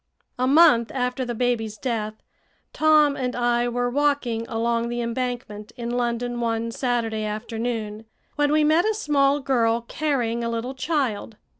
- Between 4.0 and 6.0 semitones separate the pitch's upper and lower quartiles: No, average, 2.8 semitones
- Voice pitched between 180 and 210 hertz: No, high, 240 Hz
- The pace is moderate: Yes, average, 150 wpm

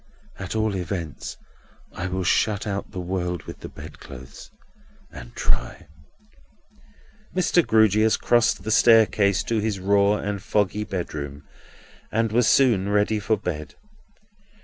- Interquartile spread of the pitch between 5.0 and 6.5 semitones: No, average, 3.2 semitones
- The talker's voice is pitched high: No, low, 100 Hz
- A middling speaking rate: No, slow, 125 wpm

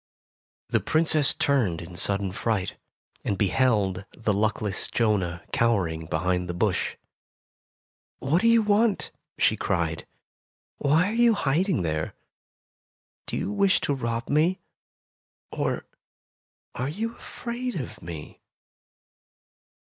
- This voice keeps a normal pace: No, slow, 120 wpm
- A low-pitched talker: Yes, low, 115 Hz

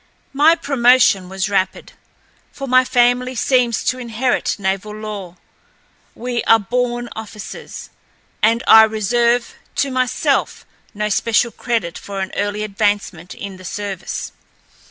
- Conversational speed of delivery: No, slow, 125 wpm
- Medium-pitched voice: No, high, 220 Hz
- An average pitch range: Yes, average, 3.5 semitones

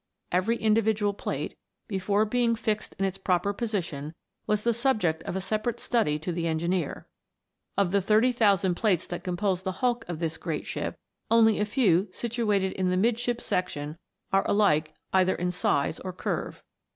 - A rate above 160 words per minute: Yes, average, 175 wpm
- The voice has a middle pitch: No, high, 195 Hz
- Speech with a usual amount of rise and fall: Yes, average, 3.7 semitones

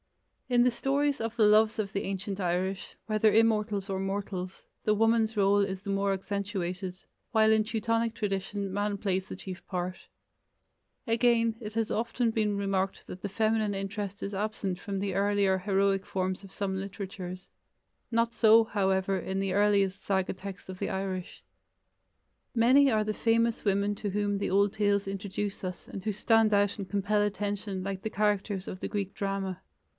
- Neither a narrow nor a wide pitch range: No, narrow, 2.0 semitones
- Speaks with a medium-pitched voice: No, high, 200 Hz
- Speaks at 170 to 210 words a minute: Yes, average, 175 wpm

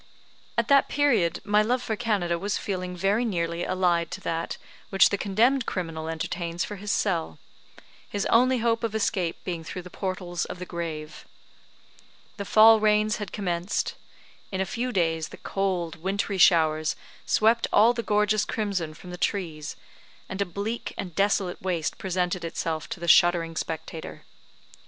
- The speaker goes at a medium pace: Yes, average, 165 wpm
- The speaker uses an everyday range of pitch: Yes, average, 3.7 semitones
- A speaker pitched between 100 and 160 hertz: No, medium, 185 Hz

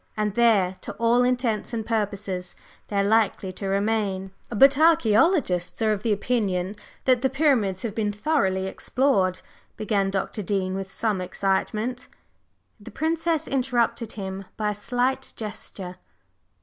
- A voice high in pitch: Yes, high, 215 Hz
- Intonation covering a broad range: No, average, 4.2 semitones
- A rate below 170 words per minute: Yes, average, 140 wpm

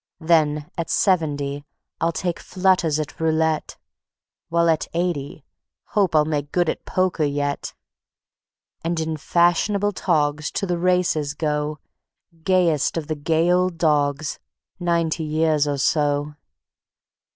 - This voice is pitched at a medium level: Yes, medium, 160 Hz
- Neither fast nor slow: No, slow, 125 wpm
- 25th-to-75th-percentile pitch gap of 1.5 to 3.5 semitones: Yes, average, 2.7 semitones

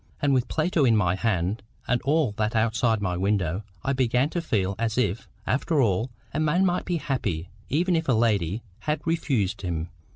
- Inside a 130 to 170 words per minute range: No, average, 190 wpm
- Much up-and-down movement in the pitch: Yes, wide, 6.6 semitones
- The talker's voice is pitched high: No, low, 115 Hz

